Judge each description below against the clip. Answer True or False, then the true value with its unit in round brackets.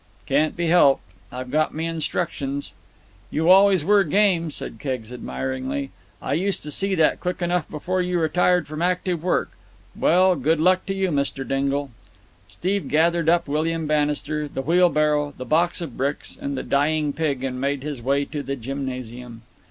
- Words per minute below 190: True (170 wpm)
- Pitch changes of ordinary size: True (4.0 semitones)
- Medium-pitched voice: True (150 Hz)